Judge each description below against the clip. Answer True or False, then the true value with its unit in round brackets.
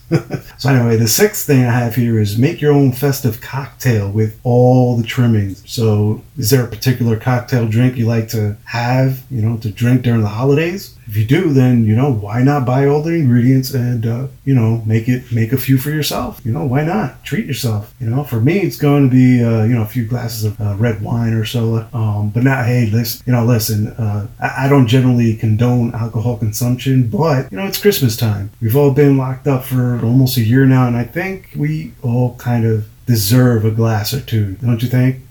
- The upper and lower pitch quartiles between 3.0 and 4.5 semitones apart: False (2.6 semitones)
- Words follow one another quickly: True (225 wpm)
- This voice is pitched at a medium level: False (120 Hz)